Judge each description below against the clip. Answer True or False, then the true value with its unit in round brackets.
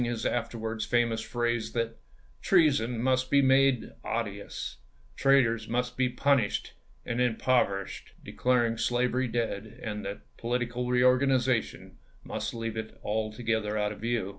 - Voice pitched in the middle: False (120 Hz)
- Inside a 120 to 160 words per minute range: True (140 wpm)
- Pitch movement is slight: True (2.0 semitones)